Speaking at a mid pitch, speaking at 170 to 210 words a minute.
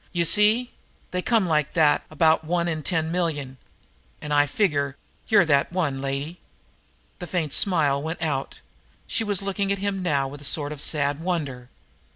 Yes: medium, 160 Hz; average, 180 wpm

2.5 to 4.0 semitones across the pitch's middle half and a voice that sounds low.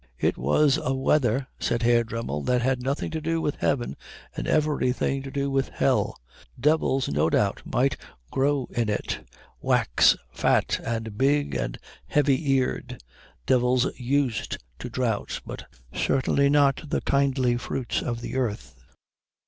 Yes: average, 2.9 semitones; low, 130 Hz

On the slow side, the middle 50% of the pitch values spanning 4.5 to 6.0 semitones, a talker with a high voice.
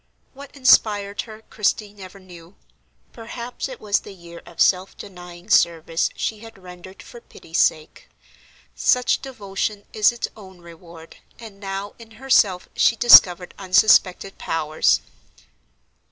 No: slow, 130 wpm; average, 3.7 semitones; high, 195 Hz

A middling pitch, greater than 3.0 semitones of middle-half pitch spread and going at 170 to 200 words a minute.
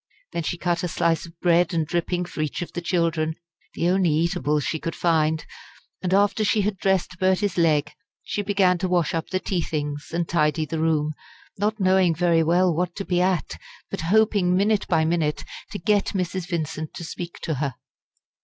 No: medium, 170 Hz; average, 2.7 semitones; average, 195 wpm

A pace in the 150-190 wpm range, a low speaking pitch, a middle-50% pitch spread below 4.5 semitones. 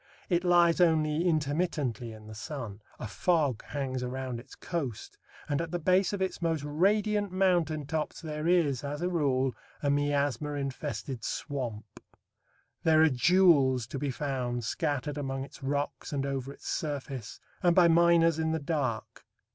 No: average, 160 wpm; medium, 145 Hz; average, 4.1 semitones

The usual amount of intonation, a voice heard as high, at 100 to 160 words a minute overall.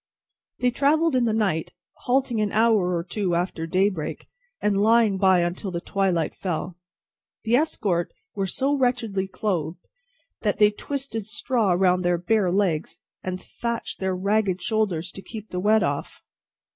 Yes: average, 3.7 semitones; high, 200 Hz; average, 155 wpm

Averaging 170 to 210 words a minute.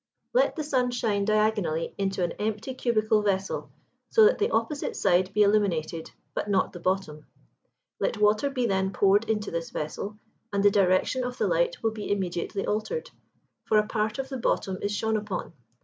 Yes: average, 180 wpm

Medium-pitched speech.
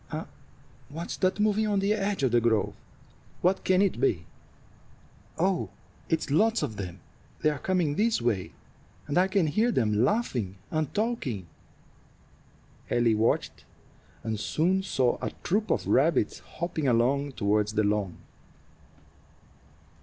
Yes: medium, 145 Hz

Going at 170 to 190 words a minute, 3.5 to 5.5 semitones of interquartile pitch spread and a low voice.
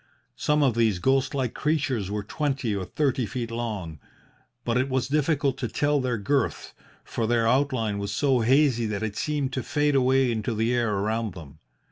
Yes: average, 185 wpm; average, 3.8 semitones; low, 120 Hz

